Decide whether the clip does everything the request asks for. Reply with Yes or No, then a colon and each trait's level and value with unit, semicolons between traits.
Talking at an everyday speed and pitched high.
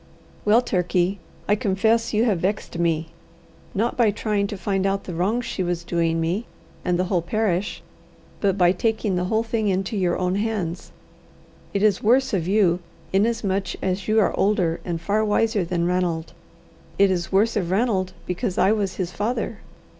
Yes: average, 175 wpm; high, 195 Hz